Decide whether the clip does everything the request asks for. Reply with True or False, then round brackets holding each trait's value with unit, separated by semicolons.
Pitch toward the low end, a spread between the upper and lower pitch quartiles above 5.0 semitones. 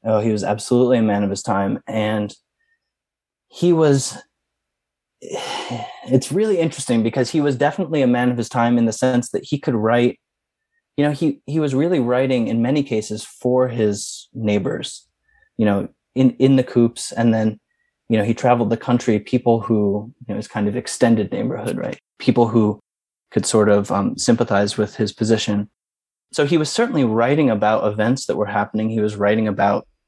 False (115 Hz; 3.7 semitones)